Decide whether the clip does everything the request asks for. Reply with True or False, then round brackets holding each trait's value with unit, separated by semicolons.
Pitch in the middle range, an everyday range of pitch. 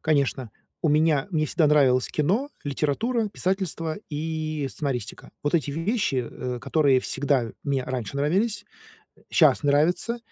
True (150 Hz; 3.2 semitones)